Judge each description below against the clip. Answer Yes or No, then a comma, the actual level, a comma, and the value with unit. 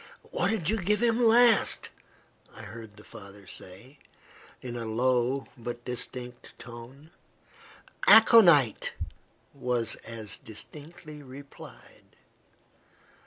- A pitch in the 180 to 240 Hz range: No, low, 125 Hz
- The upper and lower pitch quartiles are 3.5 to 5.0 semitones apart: No, wide, 5.6 semitones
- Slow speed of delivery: Yes, slow, 100 wpm